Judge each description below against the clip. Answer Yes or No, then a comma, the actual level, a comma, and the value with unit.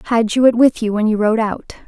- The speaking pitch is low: No, high, 225 Hz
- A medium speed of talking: No, fast, 290 wpm